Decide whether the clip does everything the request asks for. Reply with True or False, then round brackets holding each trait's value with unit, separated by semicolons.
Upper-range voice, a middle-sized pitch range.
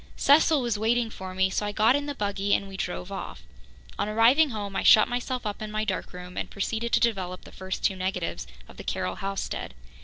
True (210 Hz; 3.5 semitones)